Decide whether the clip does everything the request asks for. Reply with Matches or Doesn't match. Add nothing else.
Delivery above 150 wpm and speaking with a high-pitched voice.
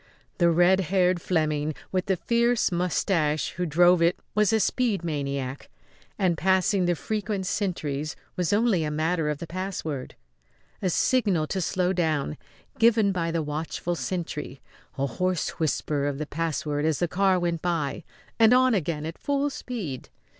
Doesn't match